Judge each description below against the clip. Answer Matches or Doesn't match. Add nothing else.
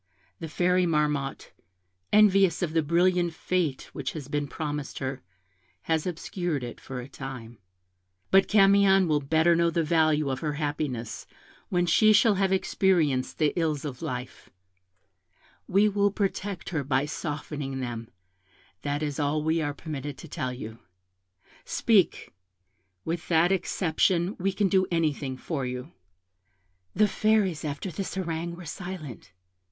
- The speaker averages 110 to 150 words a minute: Matches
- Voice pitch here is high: Doesn't match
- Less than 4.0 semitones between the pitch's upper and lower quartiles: Doesn't match